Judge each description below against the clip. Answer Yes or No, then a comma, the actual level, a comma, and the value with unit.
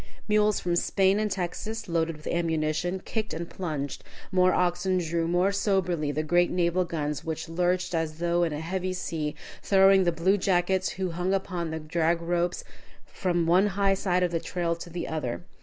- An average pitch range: No, narrow, 2.2 semitones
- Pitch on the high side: No, medium, 175 Hz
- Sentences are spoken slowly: No, average, 185 wpm